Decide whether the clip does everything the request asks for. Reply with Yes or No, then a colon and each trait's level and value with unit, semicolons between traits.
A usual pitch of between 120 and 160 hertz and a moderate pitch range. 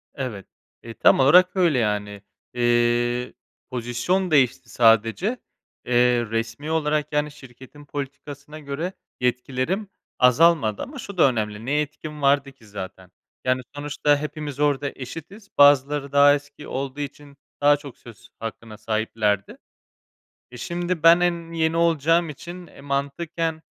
Yes: medium, 140 Hz; average, 4.3 semitones